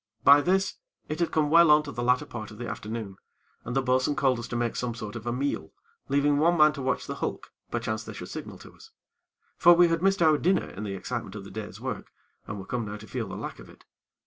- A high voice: No, low, 130 Hz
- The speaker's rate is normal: No, fast, 260 wpm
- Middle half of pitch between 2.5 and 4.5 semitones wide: No, wide, 5.5 semitones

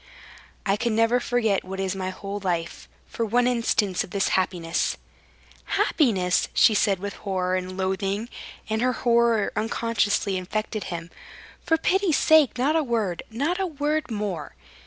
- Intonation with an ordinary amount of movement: Yes, average, 4.4 semitones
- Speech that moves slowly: No, average, 155 wpm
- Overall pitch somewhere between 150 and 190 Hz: No, high, 215 Hz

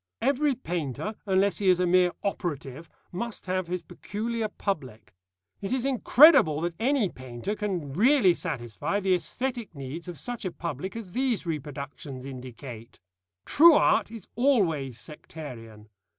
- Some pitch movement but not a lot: No, wide, 8.2 semitones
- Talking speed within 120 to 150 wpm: Yes, average, 140 wpm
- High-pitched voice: No, medium, 180 Hz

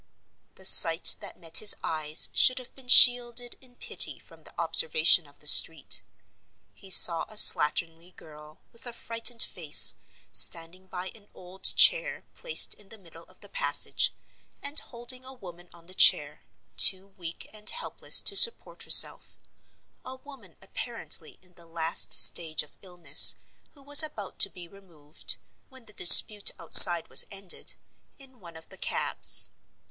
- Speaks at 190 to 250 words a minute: No, average, 155 wpm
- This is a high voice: Yes, high, 195 Hz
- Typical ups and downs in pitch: No, wide, 6.5 semitones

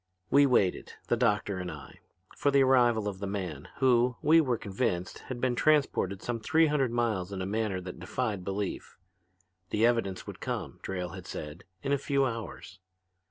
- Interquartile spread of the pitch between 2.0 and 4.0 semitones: No, average, 5.3 semitones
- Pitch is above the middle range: No, low, 110 Hz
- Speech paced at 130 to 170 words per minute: No, average, 180 wpm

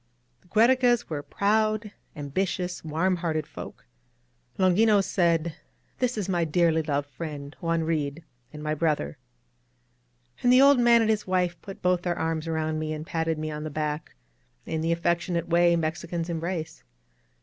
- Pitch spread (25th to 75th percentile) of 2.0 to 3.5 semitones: Yes, average, 3.2 semitones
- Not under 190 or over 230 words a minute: No, average, 160 wpm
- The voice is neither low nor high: Yes, medium, 170 Hz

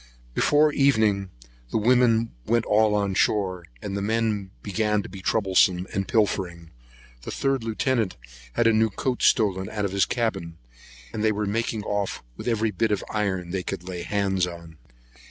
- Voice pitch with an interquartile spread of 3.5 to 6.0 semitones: No, average, 2.9 semitones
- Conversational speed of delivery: Yes, average, 175 wpm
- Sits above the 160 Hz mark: No, low, 105 Hz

